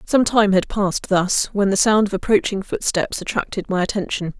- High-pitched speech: Yes, high, 200 Hz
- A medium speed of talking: Yes, average, 190 wpm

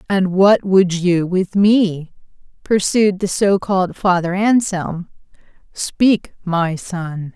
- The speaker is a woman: Yes, female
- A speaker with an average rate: No, slow, 115 wpm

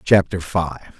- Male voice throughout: Yes, male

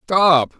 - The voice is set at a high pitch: No, medium, 165 Hz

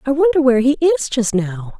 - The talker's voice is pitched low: No, very high, 255 Hz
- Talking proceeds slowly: No, fast, 235 wpm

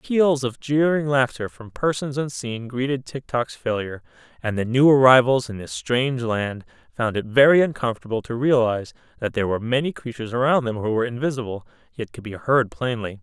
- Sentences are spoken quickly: No, average, 180 wpm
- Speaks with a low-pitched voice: Yes, low, 125 Hz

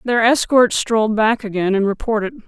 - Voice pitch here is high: Yes, high, 220 Hz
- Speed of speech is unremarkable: Yes, average, 170 wpm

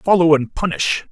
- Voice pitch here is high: No, medium, 165 Hz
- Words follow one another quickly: No, average, 160 wpm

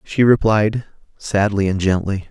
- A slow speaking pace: Yes, slow, 130 wpm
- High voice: No, low, 100 Hz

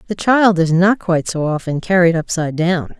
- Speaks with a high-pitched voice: No, medium, 175 Hz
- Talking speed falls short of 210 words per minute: Yes, average, 200 wpm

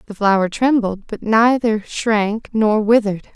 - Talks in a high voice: Yes, high, 215 Hz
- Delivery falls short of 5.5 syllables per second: Yes, 4.2 syllables/s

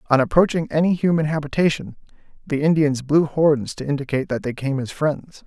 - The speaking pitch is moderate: Yes, medium, 150 Hz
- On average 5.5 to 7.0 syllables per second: Yes, 5.7 syllables/s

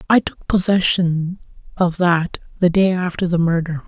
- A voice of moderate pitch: Yes, medium, 175 Hz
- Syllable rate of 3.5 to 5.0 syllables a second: Yes, 4.5 syllables/s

